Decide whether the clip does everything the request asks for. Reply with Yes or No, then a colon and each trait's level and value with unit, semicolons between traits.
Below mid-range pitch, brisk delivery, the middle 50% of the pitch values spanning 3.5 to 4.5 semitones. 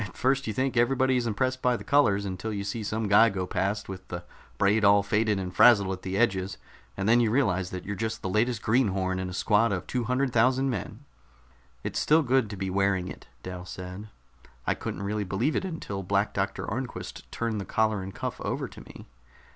Yes: low, 105 Hz; fast, 220 wpm; average, 3.8 semitones